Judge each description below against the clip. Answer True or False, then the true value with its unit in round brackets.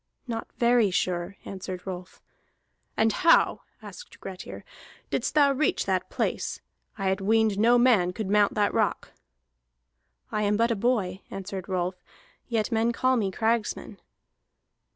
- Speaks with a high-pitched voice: True (210 Hz)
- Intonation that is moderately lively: True (3.6 semitones)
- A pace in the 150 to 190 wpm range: False (140 wpm)